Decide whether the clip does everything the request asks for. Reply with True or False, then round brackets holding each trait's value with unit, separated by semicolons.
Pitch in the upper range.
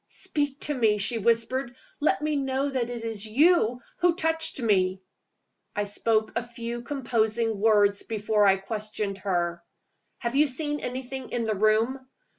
True (230 Hz)